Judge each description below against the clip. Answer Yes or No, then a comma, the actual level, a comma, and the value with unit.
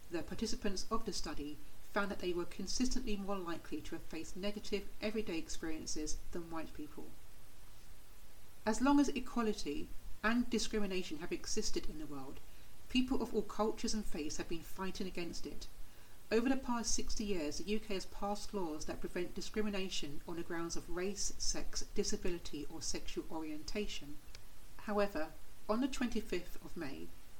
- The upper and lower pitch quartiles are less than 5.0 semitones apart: No, wide, 5.6 semitones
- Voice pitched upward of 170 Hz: Yes, high, 190 Hz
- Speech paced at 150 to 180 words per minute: Yes, average, 160 wpm